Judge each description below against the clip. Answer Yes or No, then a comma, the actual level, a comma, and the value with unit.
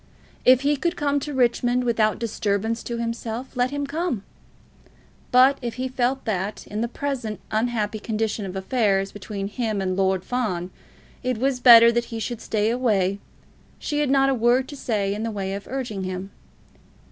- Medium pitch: No, high, 230 Hz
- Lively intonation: No, average, 3.7 semitones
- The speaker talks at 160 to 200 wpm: Yes, average, 180 wpm